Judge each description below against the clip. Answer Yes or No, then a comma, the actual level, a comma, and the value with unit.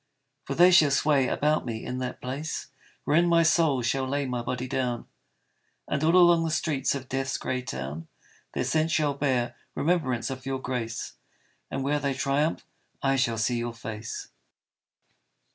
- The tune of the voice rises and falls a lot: No, average, 3.5 semitones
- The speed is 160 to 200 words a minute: Yes, average, 165 wpm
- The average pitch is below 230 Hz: Yes, low, 135 Hz